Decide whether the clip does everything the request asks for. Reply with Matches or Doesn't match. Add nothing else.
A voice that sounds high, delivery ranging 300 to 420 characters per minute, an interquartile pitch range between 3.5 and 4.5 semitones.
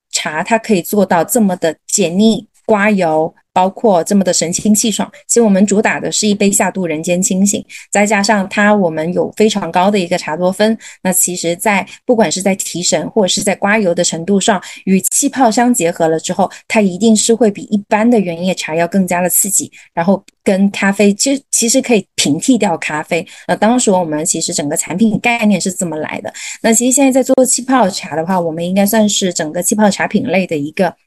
Matches